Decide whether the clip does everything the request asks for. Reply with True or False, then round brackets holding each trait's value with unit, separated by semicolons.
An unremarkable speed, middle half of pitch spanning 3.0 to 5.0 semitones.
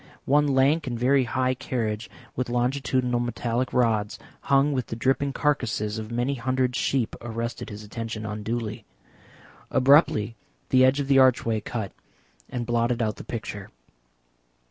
False (145 wpm; 2.6 semitones)